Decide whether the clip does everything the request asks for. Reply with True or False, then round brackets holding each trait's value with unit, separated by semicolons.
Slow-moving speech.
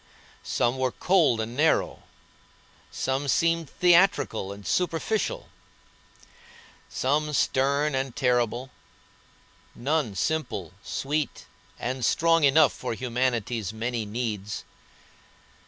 True (90 wpm)